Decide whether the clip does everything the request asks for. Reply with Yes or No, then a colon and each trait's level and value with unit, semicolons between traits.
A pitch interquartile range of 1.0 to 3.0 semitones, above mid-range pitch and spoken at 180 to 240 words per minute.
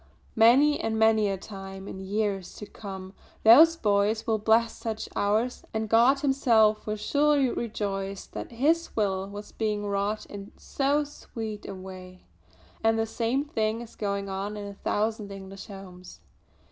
No: narrow, 2.5 semitones; high, 215 Hz; average, 160 wpm